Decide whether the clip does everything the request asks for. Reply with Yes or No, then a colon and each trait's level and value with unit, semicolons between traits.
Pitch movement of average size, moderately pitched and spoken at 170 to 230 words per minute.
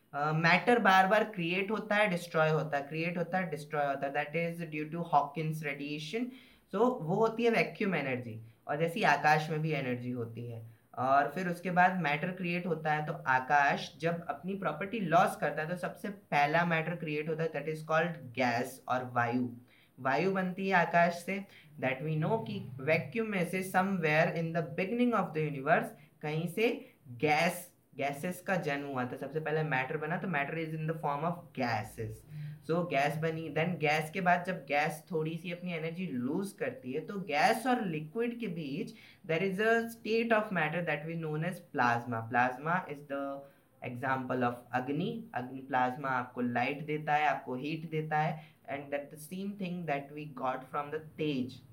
Yes: average, 4.2 semitones; medium, 155 Hz; fast, 190 wpm